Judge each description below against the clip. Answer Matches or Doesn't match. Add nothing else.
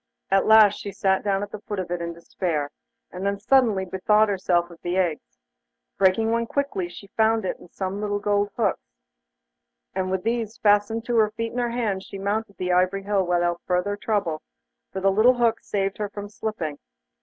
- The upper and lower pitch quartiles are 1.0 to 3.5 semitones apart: Matches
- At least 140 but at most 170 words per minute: Doesn't match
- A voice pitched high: Matches